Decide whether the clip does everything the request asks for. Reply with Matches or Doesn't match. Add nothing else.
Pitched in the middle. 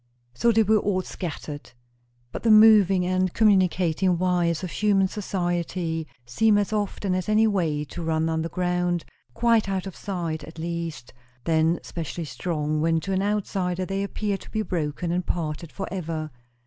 Matches